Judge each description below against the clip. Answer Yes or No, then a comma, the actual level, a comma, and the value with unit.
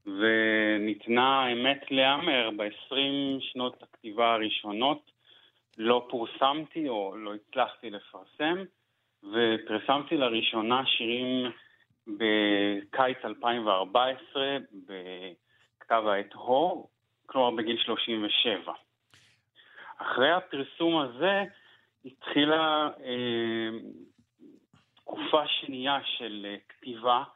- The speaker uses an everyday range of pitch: Yes, average, 3.6 semitones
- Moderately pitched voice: No, low, 125 Hz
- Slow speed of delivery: Yes, slow, 75 wpm